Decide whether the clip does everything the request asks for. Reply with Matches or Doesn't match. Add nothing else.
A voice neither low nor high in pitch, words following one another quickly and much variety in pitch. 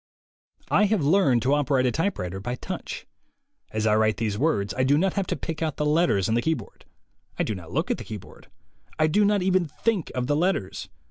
Matches